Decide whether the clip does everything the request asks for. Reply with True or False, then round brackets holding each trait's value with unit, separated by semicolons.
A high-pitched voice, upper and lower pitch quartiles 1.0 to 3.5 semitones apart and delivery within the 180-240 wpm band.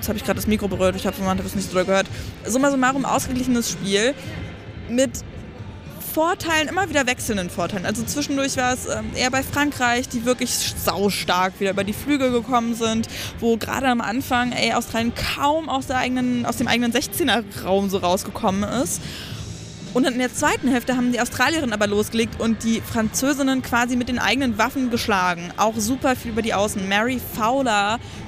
False (240 Hz; 3.9 semitones; 185 wpm)